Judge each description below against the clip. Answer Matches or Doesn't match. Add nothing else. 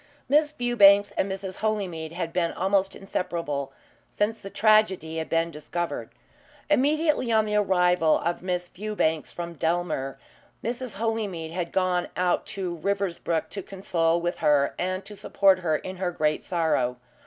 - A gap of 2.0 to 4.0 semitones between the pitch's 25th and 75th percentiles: Matches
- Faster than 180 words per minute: Doesn't match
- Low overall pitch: Doesn't match